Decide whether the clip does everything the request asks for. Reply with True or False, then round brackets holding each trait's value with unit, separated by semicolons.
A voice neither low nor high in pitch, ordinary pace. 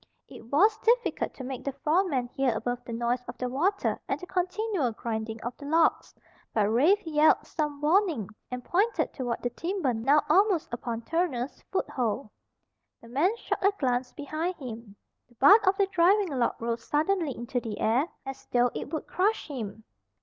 False (275 Hz; 180 wpm)